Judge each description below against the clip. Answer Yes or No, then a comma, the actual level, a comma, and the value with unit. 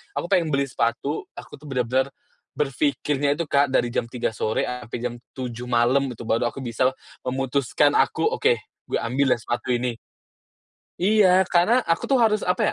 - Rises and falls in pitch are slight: No, average, 4.7 semitones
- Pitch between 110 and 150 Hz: Yes, low, 135 Hz